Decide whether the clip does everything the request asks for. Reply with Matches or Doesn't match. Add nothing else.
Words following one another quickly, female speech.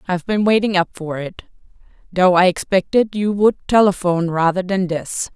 Doesn't match